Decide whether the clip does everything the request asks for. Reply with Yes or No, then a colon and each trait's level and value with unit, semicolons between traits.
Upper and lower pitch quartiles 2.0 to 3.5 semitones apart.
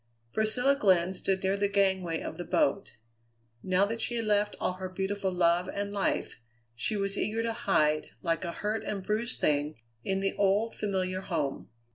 Yes: narrow, 2.4 semitones